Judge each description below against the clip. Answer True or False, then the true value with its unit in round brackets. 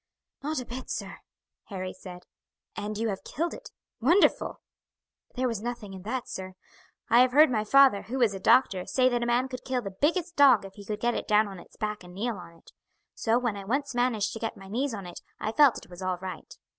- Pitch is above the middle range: True (225 Hz)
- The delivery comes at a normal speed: False (235 wpm)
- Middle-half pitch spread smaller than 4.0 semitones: False (4.6 semitones)